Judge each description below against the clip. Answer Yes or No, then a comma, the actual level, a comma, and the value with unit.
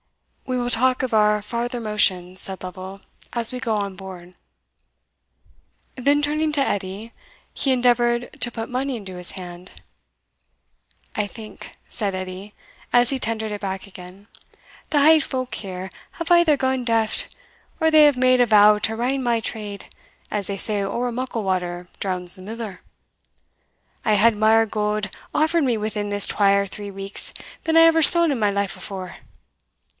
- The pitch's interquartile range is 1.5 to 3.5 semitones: No, average, 4.2 semitones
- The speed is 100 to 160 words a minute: No, average, 170 wpm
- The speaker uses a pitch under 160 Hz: No, high, 215 Hz